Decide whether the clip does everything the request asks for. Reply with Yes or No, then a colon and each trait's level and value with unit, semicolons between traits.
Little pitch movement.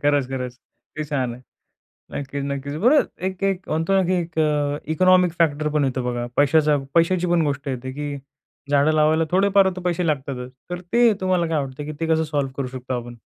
No: average, 4.2 semitones